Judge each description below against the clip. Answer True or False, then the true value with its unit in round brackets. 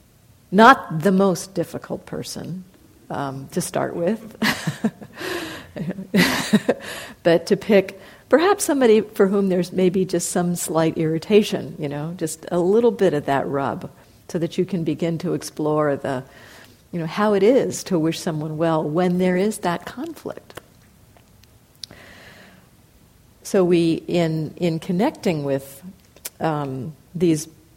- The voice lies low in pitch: False (175 Hz)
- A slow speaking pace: True (130 wpm)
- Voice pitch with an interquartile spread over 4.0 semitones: False (3.7 semitones)